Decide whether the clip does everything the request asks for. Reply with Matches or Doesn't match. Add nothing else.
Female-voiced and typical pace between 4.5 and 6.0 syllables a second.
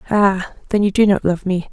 Matches